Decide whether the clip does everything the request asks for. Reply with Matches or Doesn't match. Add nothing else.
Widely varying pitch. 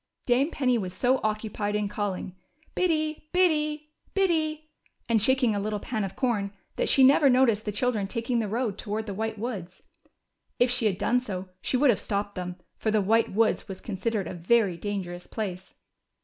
Doesn't match